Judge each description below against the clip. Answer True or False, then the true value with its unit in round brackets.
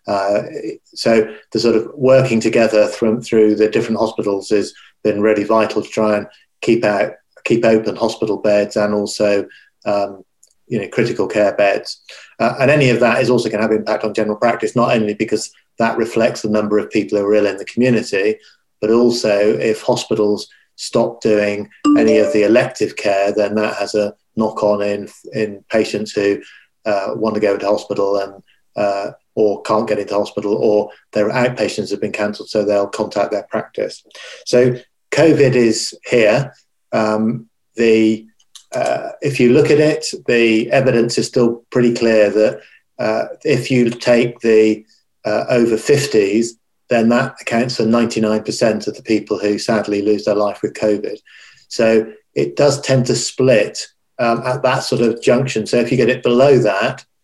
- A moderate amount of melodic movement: False (2.3 semitones)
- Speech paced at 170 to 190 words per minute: True (175 wpm)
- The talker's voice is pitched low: True (110 Hz)